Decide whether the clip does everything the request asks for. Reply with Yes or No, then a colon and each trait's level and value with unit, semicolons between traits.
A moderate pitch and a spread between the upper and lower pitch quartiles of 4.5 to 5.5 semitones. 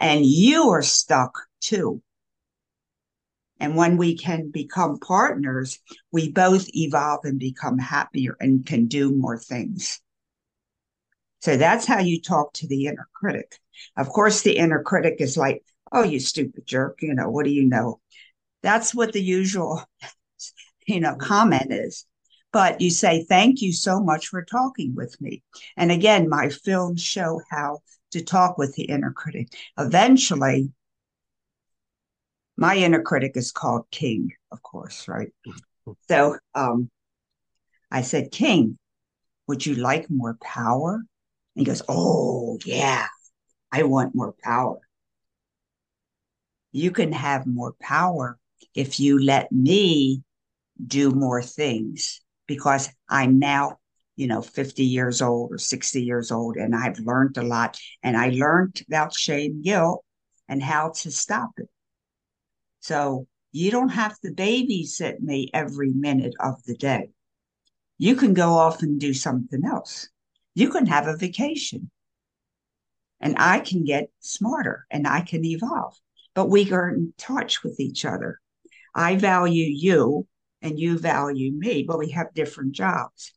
Yes: medium, 150 Hz; average, 5.0 semitones